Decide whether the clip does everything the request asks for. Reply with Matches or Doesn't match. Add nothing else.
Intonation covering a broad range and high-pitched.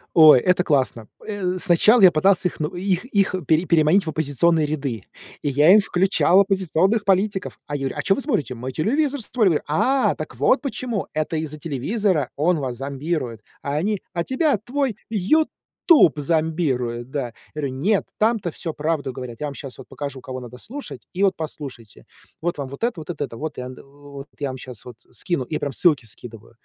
Doesn't match